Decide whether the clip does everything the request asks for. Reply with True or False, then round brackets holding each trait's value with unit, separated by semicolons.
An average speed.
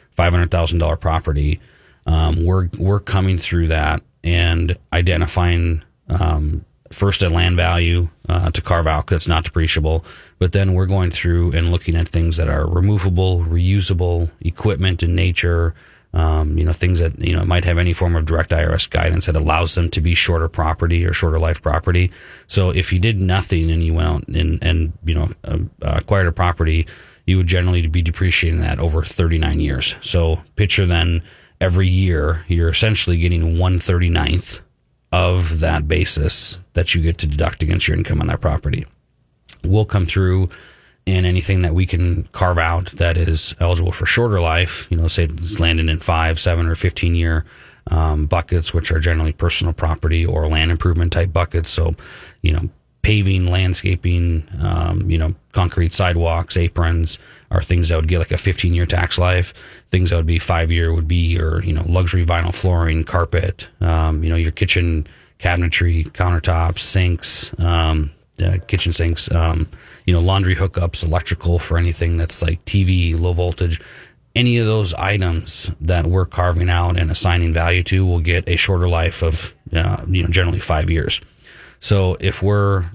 True (175 wpm)